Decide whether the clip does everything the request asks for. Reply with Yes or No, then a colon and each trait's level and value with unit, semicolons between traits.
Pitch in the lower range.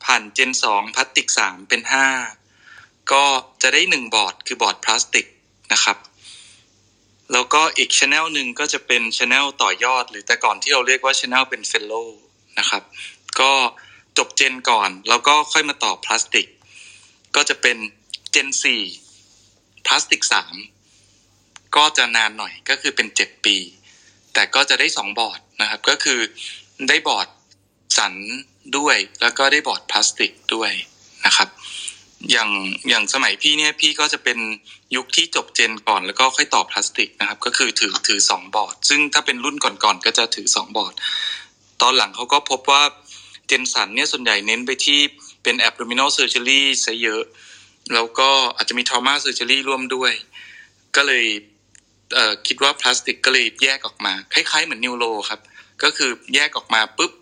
Yes: low, 125 Hz